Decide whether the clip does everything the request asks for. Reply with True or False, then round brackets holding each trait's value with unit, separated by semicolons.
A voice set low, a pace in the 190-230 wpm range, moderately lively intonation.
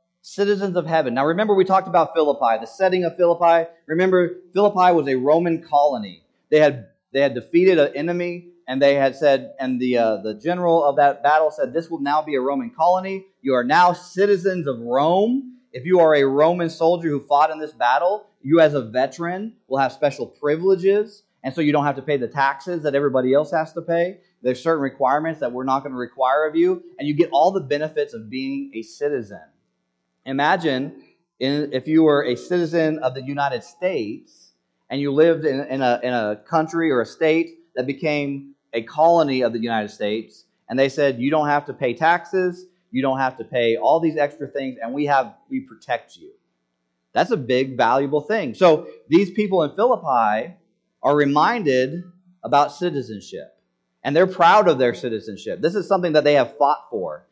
False (155 Hz; 200 wpm; 4.7 semitones)